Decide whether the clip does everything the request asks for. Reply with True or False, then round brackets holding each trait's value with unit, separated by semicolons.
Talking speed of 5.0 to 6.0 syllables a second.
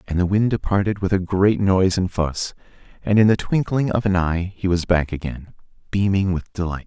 True (5.3 syllables/s)